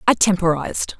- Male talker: No, female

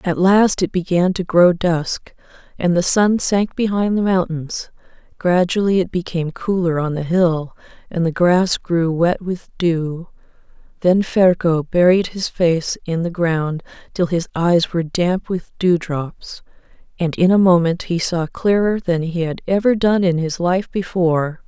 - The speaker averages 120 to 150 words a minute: No, average, 165 wpm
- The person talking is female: Yes, female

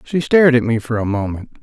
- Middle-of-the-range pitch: No, low, 125 Hz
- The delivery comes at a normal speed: No, fast, 260 wpm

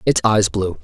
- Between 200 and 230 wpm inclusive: Yes, fast, 215 wpm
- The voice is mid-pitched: No, low, 100 Hz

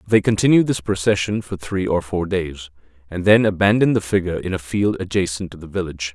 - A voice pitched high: No, very low, 95 Hz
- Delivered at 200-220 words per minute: Yes, fast, 205 wpm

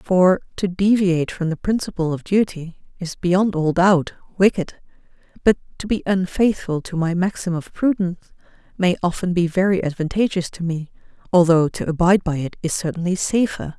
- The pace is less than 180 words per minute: Yes, average, 160 wpm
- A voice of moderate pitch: Yes, medium, 180 Hz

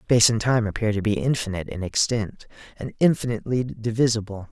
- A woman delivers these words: No, male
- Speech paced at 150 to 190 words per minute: Yes, average, 160 wpm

